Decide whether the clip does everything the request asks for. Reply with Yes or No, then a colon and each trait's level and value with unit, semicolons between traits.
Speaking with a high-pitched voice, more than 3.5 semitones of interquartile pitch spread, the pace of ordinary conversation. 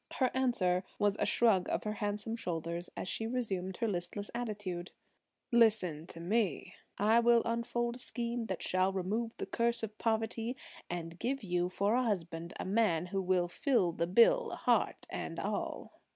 Yes: high, 205 Hz; average, 4.6 semitones; average, 170 wpm